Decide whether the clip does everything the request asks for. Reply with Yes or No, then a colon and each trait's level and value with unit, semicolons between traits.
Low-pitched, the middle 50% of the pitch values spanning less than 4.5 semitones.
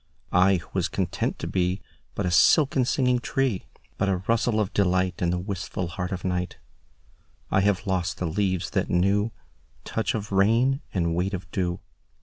Yes: very low, 95 Hz; average, 2.9 semitones